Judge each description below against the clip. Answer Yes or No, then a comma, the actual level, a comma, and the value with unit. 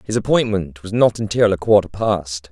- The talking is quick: No, average, 190 wpm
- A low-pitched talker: Yes, low, 100 Hz